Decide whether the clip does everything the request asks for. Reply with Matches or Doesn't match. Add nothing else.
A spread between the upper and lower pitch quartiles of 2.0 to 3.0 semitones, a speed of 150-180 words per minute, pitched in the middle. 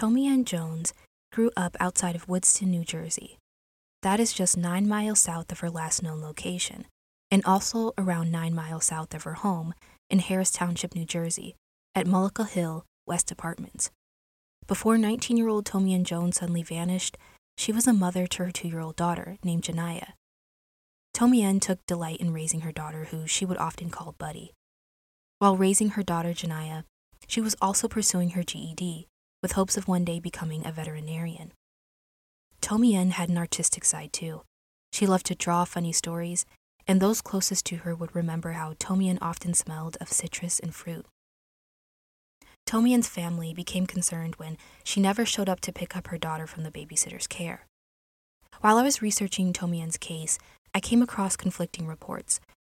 Matches